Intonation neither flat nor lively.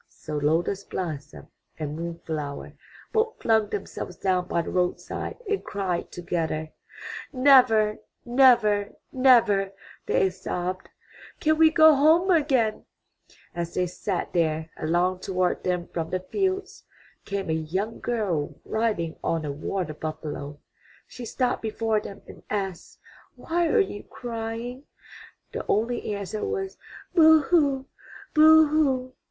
No: wide, 7.2 semitones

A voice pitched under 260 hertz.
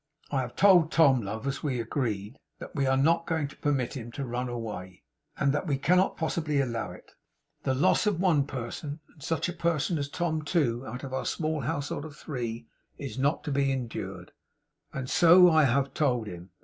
Yes: medium, 140 Hz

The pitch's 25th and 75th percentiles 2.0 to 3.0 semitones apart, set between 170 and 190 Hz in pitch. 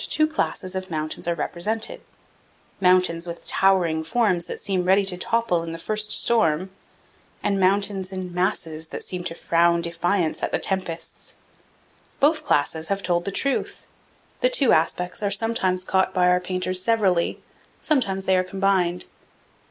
Yes: narrow, 2.6 semitones; medium, 185 Hz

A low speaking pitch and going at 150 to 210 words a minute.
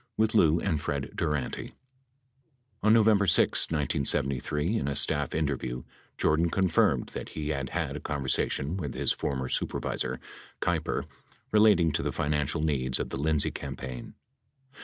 No: very low, 75 Hz; average, 140 wpm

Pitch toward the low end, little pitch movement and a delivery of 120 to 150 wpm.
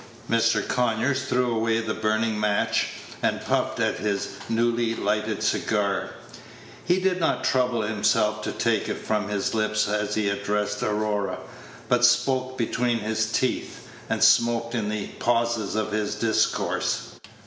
Yes: low, 110 Hz; narrow, 2.0 semitones; average, 145 wpm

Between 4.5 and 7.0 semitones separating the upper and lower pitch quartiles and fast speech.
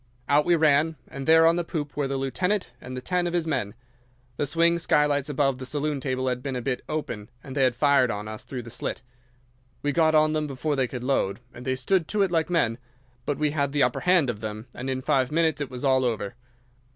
No: average, 3.7 semitones; fast, 240 wpm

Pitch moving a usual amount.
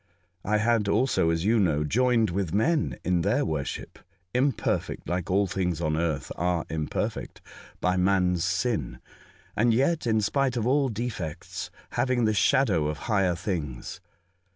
No: wide, 5.7 semitones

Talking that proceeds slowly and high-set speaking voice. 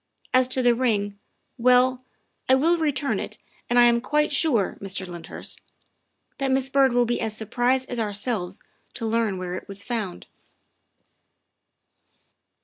No: average, 150 wpm; high, 240 Hz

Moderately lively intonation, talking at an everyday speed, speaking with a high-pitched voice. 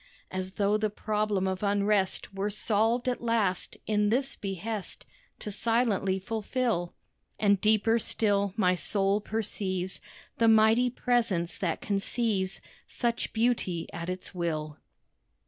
No: average, 3.0 semitones; slow, 125 wpm; high, 205 Hz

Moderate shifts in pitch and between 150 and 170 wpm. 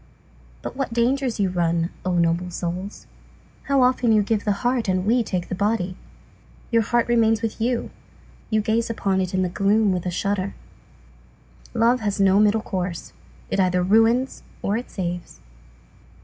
Yes: average, 3.9 semitones; average, 165 wpm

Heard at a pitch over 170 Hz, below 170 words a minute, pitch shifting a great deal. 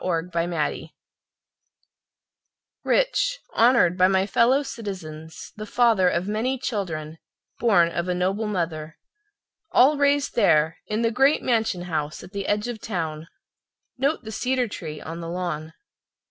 Yes: high, 190 Hz; slow, 135 wpm; wide, 5.9 semitones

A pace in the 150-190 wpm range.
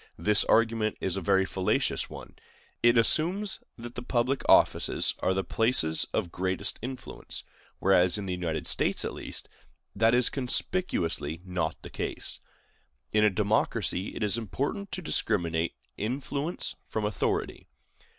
No: average, 140 wpm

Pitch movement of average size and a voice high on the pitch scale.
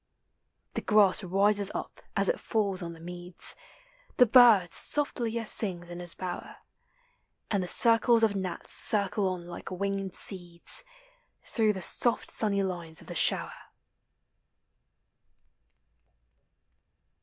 Yes: average, 3.7 semitones; high, 195 Hz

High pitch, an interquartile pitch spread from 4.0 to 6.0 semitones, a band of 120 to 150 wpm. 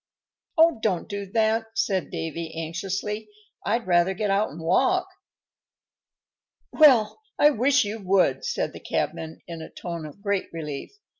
Yes: high, 200 Hz; average, 4.8 semitones; average, 145 wpm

